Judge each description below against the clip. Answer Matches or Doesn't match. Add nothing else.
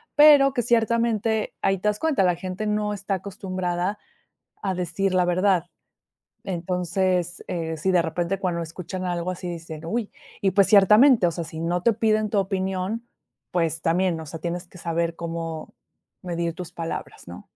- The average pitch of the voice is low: Doesn't match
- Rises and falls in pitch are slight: Doesn't match